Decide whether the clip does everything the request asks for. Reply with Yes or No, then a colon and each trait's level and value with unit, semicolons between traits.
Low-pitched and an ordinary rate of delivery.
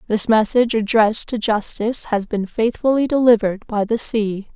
No: high, 220 Hz; average, 160 wpm